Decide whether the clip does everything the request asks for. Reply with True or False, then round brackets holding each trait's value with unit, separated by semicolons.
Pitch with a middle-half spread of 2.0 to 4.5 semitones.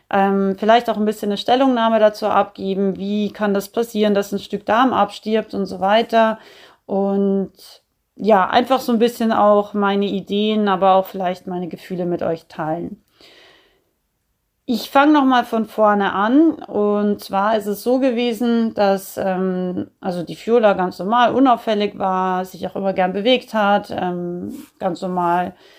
True (2.8 semitones)